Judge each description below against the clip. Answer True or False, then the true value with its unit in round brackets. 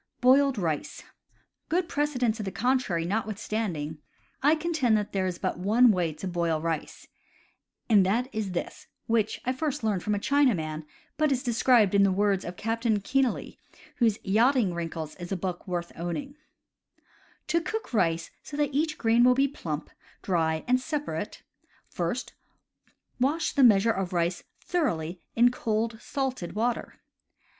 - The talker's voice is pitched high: True (220 Hz)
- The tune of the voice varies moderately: False (6.4 semitones)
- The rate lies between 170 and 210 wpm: False (160 wpm)